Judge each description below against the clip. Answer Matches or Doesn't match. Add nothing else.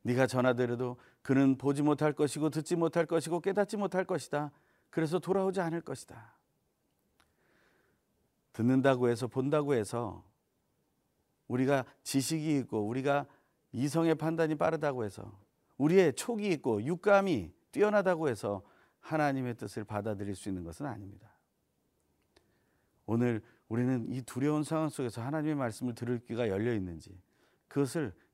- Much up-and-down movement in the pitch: Doesn't match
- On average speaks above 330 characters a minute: Doesn't match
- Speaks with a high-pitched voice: Doesn't match